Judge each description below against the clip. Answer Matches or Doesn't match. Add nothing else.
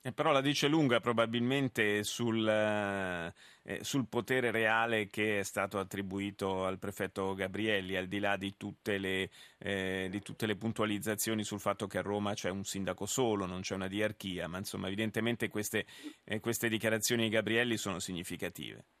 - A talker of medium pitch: Doesn't match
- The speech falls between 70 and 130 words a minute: Doesn't match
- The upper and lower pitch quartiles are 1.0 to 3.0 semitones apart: Matches